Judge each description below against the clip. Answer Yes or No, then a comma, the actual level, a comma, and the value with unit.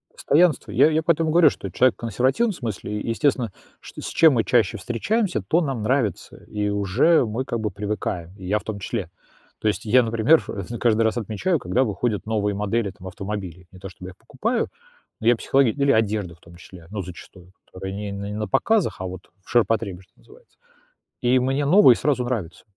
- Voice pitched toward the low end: Yes, low, 110 Hz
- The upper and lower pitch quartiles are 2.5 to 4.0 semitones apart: No, average, 5.0 semitones